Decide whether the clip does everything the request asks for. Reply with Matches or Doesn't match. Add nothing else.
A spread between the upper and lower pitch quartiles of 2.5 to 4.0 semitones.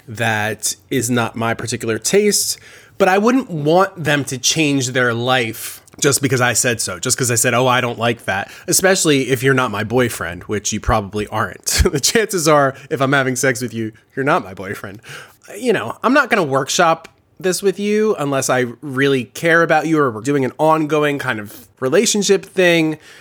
Doesn't match